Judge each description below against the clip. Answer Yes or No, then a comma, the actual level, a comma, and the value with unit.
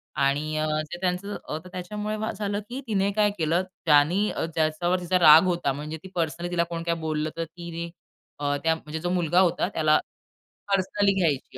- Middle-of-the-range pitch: Yes, medium, 170 Hz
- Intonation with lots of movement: No, average, 3.1 semitones